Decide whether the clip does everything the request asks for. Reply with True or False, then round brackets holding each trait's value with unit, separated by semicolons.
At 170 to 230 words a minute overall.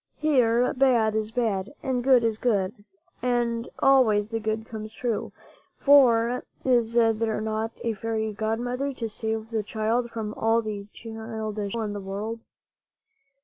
False (145 wpm)